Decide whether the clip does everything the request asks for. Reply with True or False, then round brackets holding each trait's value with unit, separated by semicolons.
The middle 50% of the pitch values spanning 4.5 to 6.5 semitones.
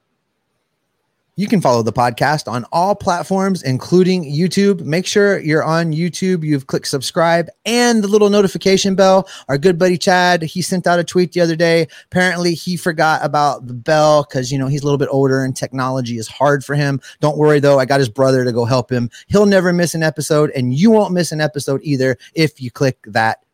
True (5.0 semitones)